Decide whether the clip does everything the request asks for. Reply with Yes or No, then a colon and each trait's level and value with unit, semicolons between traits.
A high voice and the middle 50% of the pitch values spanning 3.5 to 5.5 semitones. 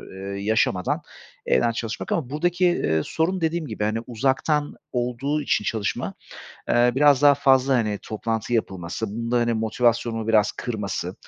No: low, 115 Hz; average, 4.5 semitones